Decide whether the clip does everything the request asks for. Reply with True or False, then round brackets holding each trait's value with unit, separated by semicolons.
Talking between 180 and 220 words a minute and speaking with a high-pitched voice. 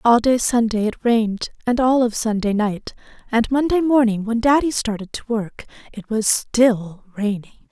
False (170 wpm; 230 Hz)